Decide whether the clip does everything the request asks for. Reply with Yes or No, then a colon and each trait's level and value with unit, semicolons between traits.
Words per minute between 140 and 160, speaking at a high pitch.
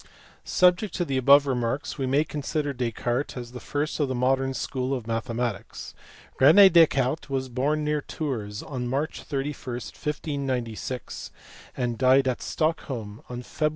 No: average, 155 wpm; low, 135 Hz